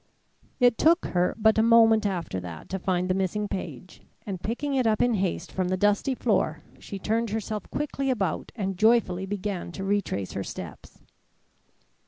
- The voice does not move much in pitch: No, average, 3.6 semitones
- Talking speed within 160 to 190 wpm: Yes, average, 175 wpm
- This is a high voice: Yes, high, 205 Hz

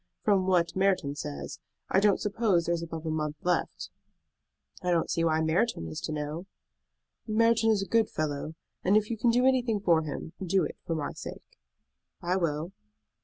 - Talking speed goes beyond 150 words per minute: Yes, average, 185 wpm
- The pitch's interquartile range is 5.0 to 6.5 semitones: No, average, 4.6 semitones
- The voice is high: No, medium, 175 Hz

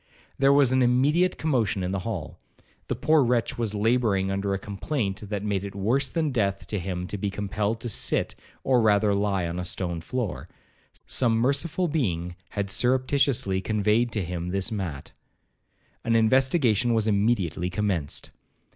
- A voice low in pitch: Yes, low, 105 Hz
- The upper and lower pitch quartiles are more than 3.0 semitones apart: Yes, average, 4.4 semitones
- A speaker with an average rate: Yes, average, 165 wpm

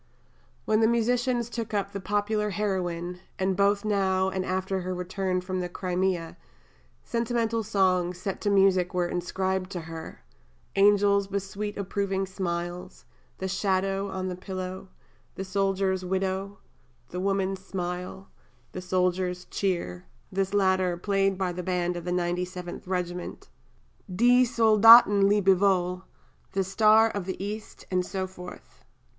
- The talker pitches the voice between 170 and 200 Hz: Yes, high, 190 Hz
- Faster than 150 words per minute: No, average, 140 wpm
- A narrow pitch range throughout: Yes, narrow, 1.8 semitones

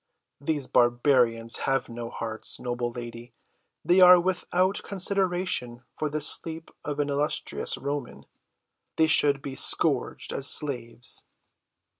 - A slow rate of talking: Yes, slow, 120 wpm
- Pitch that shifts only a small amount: No, average, 5.0 semitones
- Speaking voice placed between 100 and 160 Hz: Yes, medium, 140 Hz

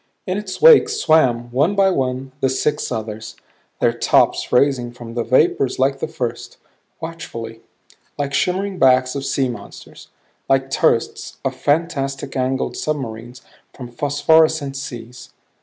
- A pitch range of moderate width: Yes, average, 4.1 semitones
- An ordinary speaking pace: No, slow, 130 wpm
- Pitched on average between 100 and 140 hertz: Yes, low, 135 Hz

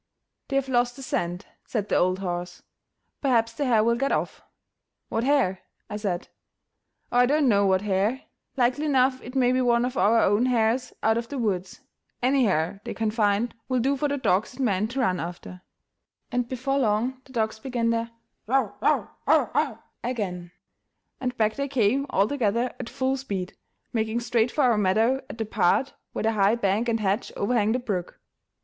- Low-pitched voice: No, high, 230 Hz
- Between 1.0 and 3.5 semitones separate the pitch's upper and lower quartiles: No, average, 3.9 semitones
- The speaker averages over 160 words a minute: Yes, average, 195 wpm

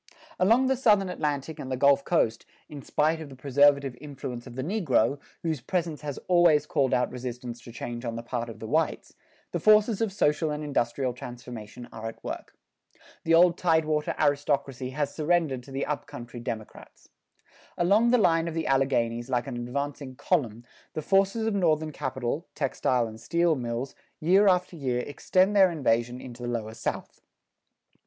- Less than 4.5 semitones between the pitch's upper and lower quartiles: No, average, 5.3 semitones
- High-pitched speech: No, medium, 140 Hz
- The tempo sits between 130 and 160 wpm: No, average, 175 wpm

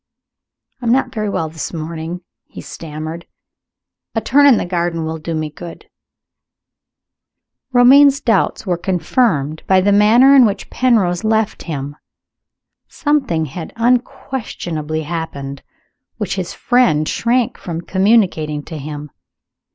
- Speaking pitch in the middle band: Yes, medium, 175 Hz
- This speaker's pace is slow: Yes, slow, 130 wpm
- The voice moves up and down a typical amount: No, wide, 6.8 semitones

